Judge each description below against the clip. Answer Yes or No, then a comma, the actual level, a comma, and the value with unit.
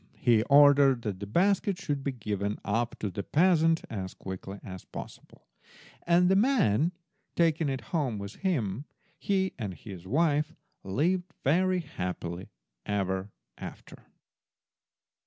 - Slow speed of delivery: Yes, slow, 130 wpm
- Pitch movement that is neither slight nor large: No, wide, 9.0 semitones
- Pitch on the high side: No, low, 135 Hz